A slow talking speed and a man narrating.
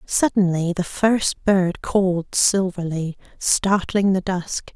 No: slow, 115 wpm; female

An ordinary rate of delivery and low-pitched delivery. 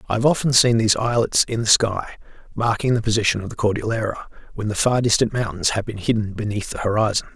No: fast, 210 wpm; low, 110 Hz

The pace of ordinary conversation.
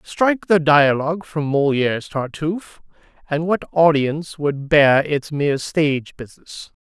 No: slow, 130 wpm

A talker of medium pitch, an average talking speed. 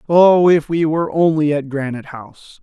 Yes: medium, 155 Hz; average, 185 wpm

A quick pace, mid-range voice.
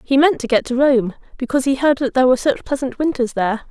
No: fast, 260 wpm; very high, 260 Hz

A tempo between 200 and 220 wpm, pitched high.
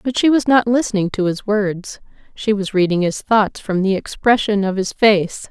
Yes: fast, 205 wpm; high, 205 Hz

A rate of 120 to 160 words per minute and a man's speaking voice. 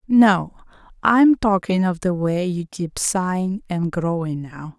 No: average, 150 wpm; female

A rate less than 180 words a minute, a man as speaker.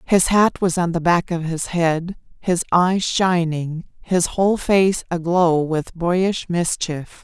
No: average, 160 wpm; female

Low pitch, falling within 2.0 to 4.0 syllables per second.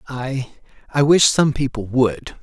Yes: low, 130 Hz; 3.8 syllables/s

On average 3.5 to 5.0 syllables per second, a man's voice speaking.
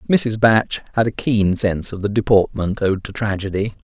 Yes: 4.9 syllables/s; male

